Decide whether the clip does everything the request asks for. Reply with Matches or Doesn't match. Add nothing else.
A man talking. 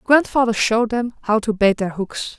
Doesn't match